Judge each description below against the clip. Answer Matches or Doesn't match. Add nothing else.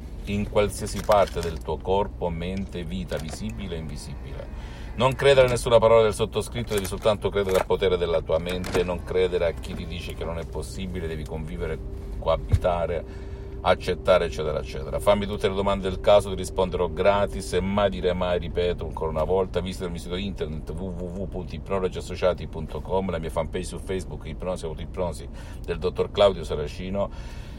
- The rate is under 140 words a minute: Doesn't match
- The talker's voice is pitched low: Matches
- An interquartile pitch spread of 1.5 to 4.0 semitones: Matches